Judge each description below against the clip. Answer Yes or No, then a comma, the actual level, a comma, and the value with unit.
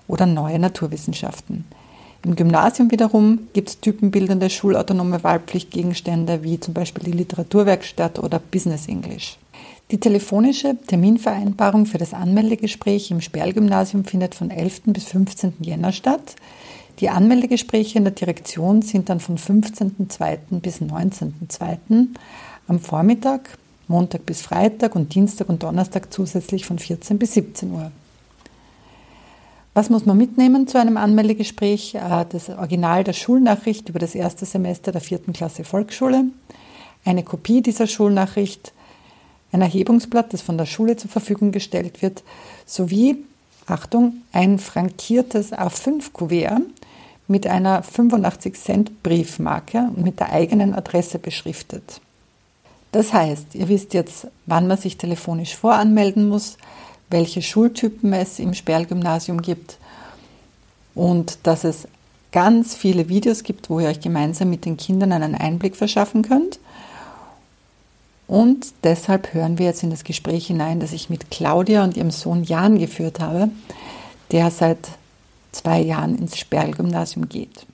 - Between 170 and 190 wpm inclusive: No, average, 130 wpm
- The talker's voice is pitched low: No, high, 190 Hz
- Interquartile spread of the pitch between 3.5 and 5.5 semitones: Yes, average, 3.8 semitones